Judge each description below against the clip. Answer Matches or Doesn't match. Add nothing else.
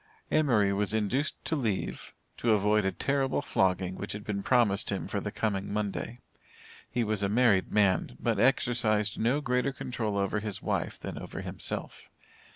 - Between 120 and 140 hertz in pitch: Doesn't match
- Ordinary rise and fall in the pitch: Matches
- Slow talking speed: Doesn't match